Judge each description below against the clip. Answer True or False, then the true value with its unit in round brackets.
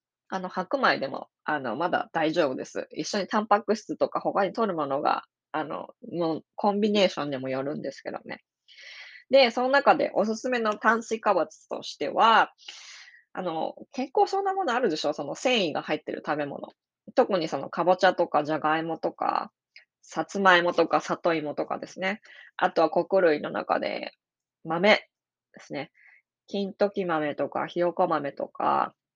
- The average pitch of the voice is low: False (195 Hz)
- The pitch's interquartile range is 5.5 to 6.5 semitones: True (5.8 semitones)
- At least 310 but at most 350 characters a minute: True (315 characters per minute)